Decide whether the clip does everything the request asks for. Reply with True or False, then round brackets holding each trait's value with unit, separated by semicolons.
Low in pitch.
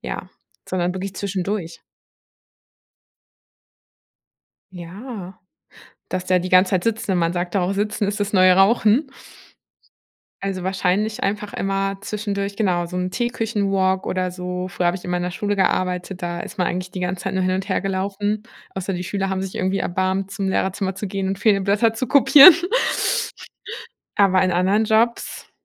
False (190 Hz)